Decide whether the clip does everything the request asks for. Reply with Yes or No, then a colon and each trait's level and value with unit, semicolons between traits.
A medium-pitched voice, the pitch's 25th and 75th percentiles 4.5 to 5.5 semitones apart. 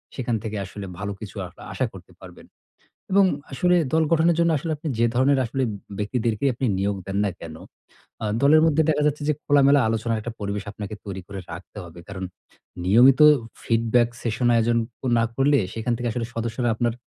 No: low, 115 Hz; average, 5.0 semitones